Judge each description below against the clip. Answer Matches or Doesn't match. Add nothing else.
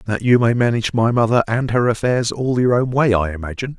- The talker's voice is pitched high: Doesn't match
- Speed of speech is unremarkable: Doesn't match